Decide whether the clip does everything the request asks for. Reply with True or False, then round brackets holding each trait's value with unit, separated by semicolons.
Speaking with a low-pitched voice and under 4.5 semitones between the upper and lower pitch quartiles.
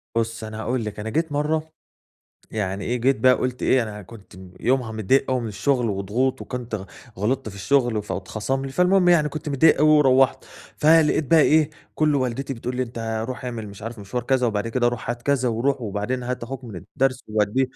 True (125 Hz; 3.7 semitones)